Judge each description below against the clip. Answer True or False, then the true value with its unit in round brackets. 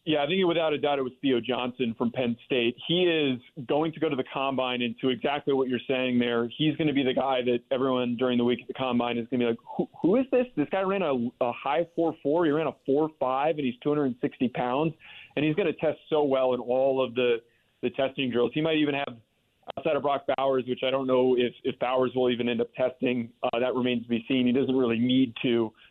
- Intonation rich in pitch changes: False (3.0 semitones)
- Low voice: True (130 Hz)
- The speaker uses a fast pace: True (270 wpm)